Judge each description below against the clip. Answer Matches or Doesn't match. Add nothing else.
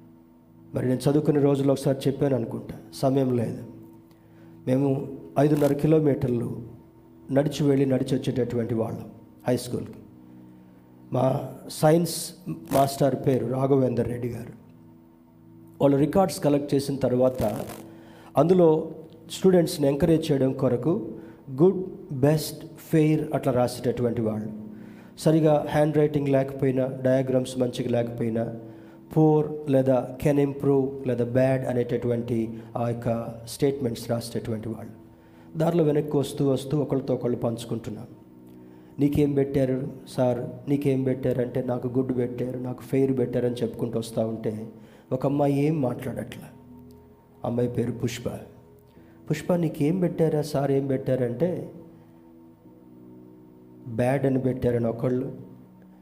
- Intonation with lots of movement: Doesn't match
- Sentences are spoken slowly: Doesn't match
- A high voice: Doesn't match